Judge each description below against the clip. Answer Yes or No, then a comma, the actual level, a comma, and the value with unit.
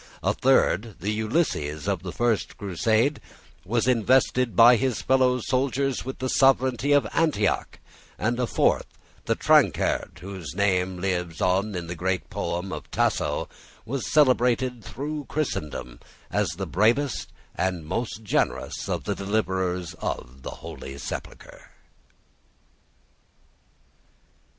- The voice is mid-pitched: No, low, 110 Hz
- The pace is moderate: No, slow, 120 wpm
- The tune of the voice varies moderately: No, wide, 5.8 semitones